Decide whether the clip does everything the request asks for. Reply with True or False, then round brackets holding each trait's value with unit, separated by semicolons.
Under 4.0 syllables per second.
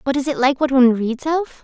False (6.8 syllables/s)